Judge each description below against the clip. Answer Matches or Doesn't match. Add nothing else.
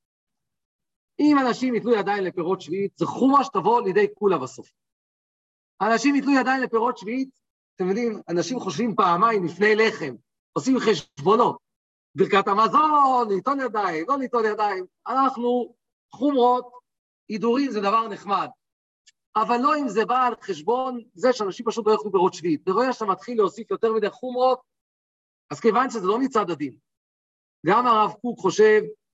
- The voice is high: Matches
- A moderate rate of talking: Matches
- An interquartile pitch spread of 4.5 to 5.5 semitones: Doesn't match